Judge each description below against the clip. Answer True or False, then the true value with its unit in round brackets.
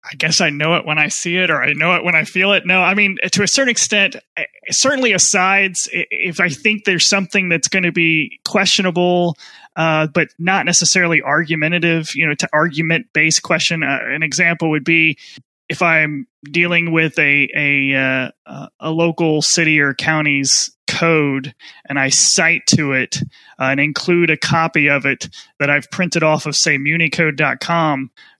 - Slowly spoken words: False (180 wpm)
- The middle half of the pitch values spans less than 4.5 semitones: True (3.1 semitones)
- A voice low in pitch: False (165 Hz)